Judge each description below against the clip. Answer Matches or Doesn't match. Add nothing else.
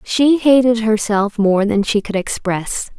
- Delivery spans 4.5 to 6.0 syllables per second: Doesn't match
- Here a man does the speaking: Doesn't match